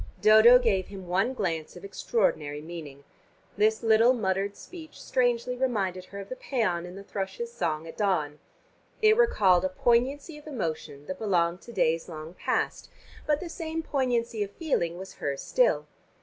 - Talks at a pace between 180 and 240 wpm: No, average, 165 wpm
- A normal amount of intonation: No, wide, 5.9 semitones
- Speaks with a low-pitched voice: No, high, 200 Hz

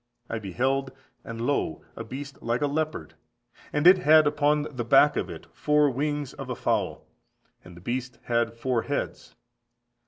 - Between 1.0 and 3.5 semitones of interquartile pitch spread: No, average, 4.1 semitones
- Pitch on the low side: Yes, low, 130 Hz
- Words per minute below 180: Yes, average, 165 wpm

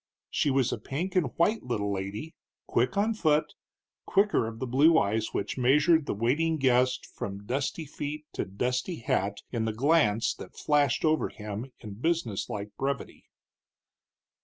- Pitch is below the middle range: Yes, low, 130 Hz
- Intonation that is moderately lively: No, wide, 5.9 semitones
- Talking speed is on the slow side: No, average, 160 wpm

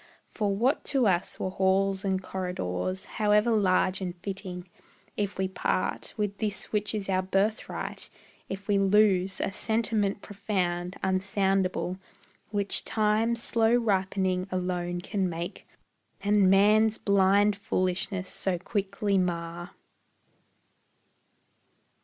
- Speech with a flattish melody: Yes, narrow, 2.0 semitones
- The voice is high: Yes, high, 195 Hz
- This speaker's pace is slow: Yes, slow, 115 wpm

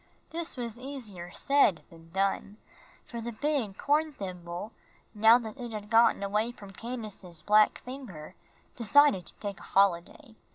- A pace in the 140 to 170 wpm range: Yes, average, 150 wpm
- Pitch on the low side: No, high, 215 Hz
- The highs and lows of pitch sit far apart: No, average, 4.2 semitones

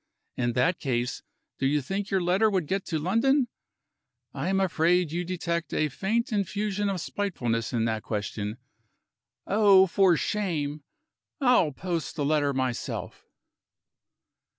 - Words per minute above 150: No, slow, 135 wpm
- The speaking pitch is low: No, medium, 175 Hz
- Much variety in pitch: Yes, wide, 5.7 semitones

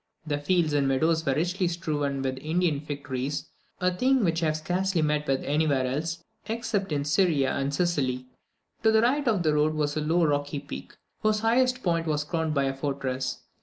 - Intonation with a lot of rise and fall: No, average, 3.9 semitones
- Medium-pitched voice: Yes, medium, 155 Hz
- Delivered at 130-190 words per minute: No, average, 200 wpm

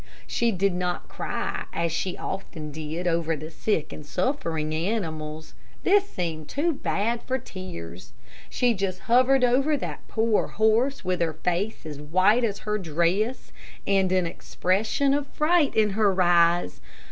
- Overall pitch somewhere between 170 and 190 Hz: Yes, medium, 185 Hz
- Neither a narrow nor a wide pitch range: No, wide, 5.8 semitones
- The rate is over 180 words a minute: No, average, 150 wpm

